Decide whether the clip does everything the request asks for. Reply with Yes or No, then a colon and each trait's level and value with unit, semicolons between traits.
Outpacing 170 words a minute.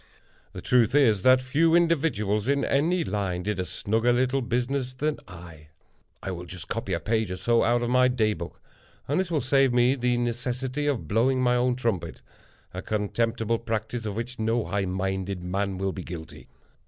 Yes: average, 185 wpm